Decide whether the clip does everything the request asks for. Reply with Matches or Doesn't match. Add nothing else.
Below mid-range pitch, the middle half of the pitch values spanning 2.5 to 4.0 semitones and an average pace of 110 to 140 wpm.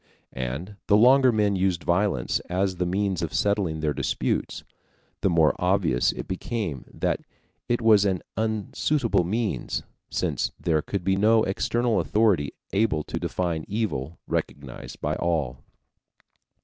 Doesn't match